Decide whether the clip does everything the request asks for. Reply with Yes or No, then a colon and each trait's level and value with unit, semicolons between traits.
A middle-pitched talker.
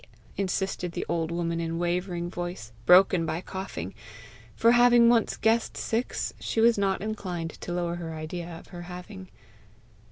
Yes: medium, 175 Hz